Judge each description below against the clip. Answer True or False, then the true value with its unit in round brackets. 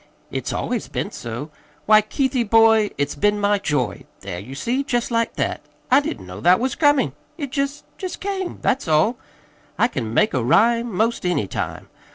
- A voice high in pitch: True (215 Hz)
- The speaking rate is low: False (185 wpm)